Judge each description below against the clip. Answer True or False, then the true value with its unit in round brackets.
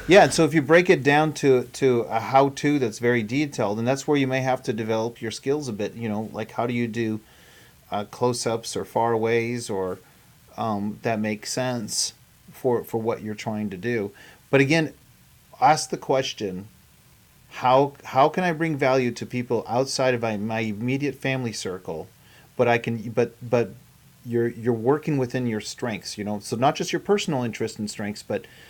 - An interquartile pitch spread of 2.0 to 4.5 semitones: True (3.2 semitones)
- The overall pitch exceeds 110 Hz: True (120 Hz)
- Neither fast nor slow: True (190 wpm)